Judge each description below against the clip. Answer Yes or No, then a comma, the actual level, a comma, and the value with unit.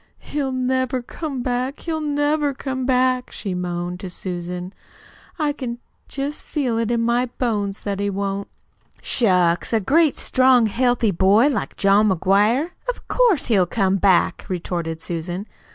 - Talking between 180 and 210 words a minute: No, average, 150 wpm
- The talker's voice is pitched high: Yes, high, 230 Hz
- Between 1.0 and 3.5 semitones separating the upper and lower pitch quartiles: No, wide, 5.5 semitones